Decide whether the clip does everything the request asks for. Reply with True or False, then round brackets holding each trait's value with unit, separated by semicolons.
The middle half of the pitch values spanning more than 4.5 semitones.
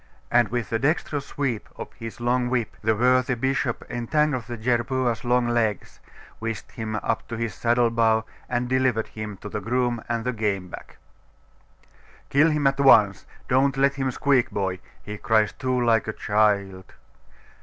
False (2.7 semitones)